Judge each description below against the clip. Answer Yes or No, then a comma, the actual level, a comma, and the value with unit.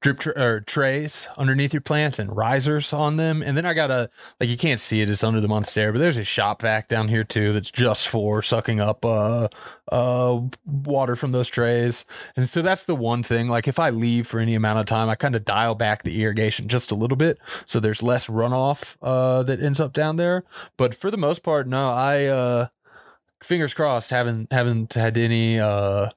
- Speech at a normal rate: No, fast, 220 wpm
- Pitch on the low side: Yes, low, 125 Hz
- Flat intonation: No, average, 4.2 semitones